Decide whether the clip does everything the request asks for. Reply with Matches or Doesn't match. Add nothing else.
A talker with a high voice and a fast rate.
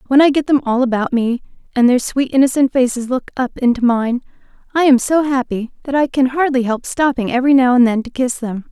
Matches